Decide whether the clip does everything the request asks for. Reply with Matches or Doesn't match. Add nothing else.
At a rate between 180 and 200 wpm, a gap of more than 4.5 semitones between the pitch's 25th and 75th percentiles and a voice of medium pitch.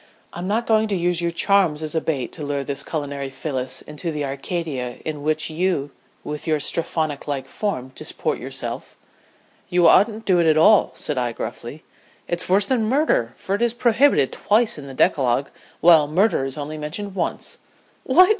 Matches